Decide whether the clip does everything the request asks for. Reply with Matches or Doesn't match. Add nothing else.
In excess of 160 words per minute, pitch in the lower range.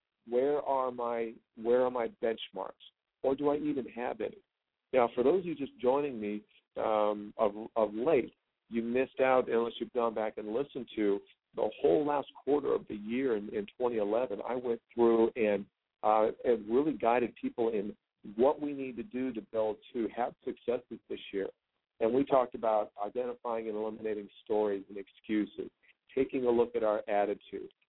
Matches